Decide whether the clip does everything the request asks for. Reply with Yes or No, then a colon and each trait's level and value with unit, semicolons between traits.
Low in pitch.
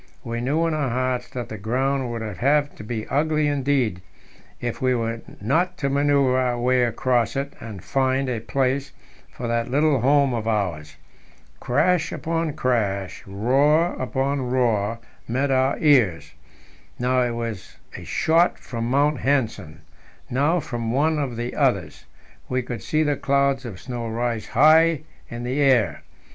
Yes: low, 130 Hz